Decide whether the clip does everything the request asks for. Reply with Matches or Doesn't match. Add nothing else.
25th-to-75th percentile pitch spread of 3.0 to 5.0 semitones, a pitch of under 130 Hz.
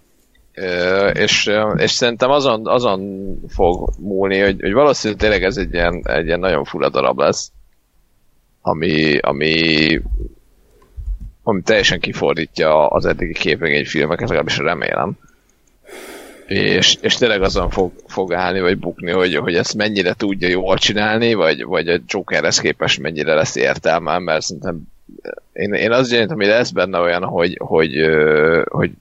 Matches